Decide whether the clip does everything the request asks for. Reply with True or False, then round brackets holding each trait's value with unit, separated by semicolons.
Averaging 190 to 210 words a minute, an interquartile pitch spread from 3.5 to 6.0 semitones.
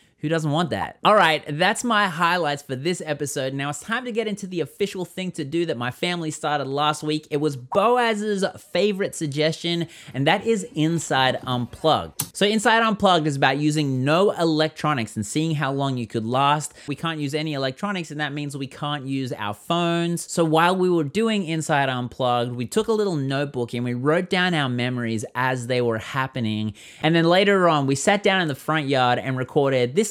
True (205 wpm; 4.6 semitones)